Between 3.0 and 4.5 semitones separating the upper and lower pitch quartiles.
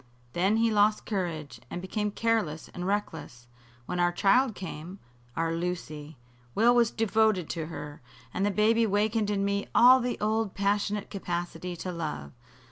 Yes: average, 3.9 semitones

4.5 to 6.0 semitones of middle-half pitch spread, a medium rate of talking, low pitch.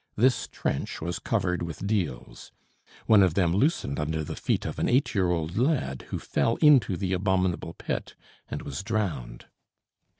Yes: average, 5.0 semitones; average, 165 wpm; very low, 95 Hz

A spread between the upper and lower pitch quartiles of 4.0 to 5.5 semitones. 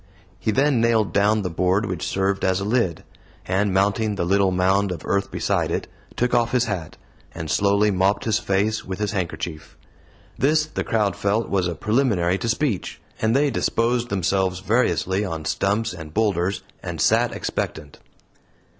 No: average, 3.3 semitones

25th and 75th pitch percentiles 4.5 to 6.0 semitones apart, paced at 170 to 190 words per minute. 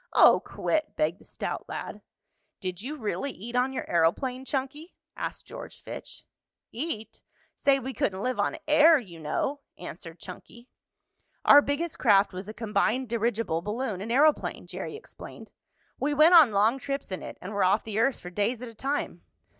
Yes: wide, 5.6 semitones; average, 175 wpm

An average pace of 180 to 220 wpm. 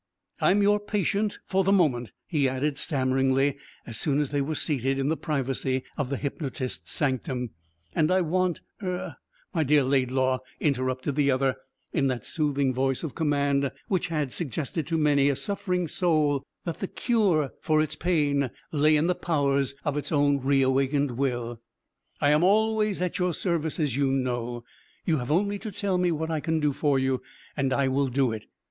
Yes: average, 185 wpm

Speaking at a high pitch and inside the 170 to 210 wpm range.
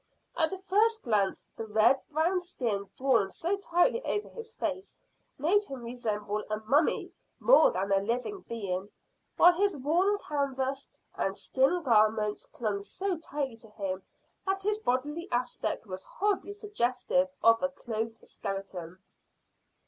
No: very high, 265 Hz; average, 140 wpm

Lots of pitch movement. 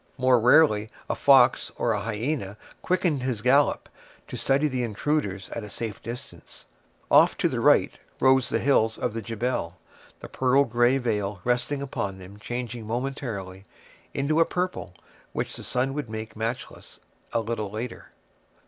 No: average, 3.9 semitones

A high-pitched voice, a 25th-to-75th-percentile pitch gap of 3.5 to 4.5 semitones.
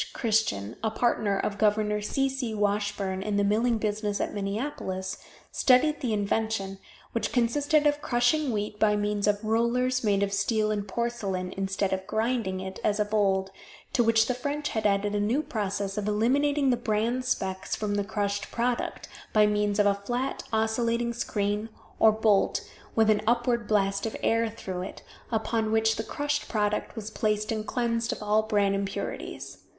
No: high, 215 Hz; narrow, 2.5 semitones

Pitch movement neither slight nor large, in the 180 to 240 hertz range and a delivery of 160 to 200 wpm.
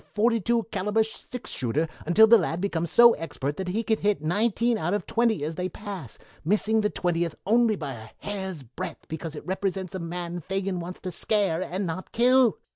Yes: average, 4.6 semitones; high, 190 Hz; average, 195 wpm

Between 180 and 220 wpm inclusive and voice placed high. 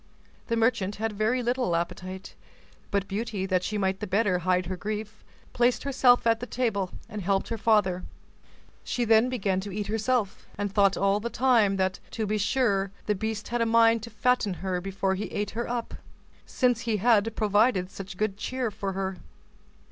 Yes: average, 185 wpm; high, 210 Hz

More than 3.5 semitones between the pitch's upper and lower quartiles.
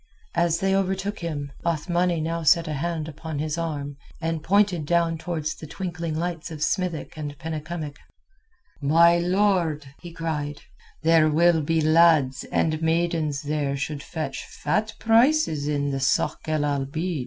No: narrow, 2.4 semitones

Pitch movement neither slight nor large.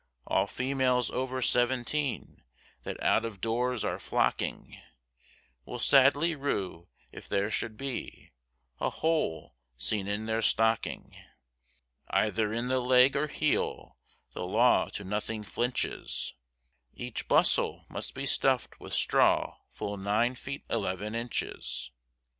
Yes: average, 3.6 semitones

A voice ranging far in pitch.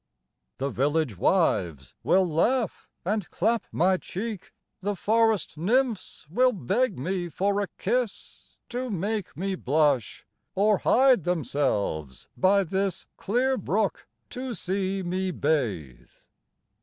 Yes: wide, 5.8 semitones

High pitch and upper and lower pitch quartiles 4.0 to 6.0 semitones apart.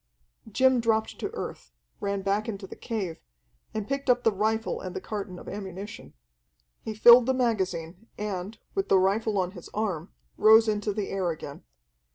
No: high, 210 Hz; average, 2.8 semitones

